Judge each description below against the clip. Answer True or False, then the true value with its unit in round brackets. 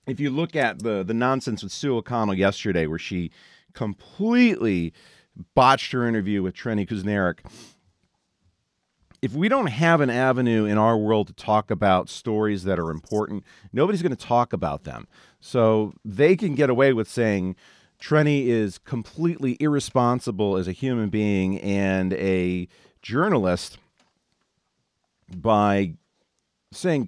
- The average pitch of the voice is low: True (110 Hz)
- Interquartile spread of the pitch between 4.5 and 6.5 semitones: True (5.1 semitones)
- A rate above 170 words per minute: False (135 wpm)